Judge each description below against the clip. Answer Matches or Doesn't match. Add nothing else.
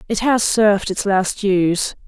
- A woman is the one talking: Matches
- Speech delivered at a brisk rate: Doesn't match